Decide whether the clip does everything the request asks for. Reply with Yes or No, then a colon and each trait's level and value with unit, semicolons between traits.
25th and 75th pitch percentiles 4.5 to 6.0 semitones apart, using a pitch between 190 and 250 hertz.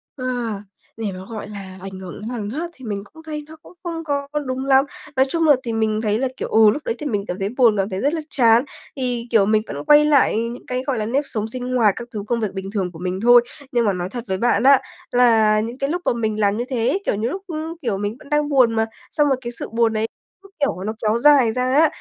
No: average, 4.1 semitones; high, 235 Hz